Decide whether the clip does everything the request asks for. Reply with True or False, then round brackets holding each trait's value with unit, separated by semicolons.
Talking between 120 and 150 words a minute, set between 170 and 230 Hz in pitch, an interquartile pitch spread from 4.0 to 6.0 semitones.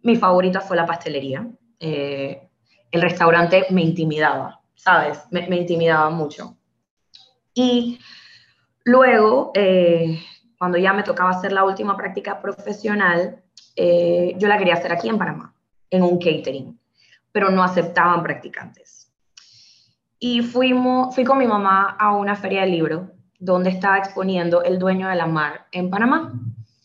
False (145 wpm; 185 Hz; 3.4 semitones)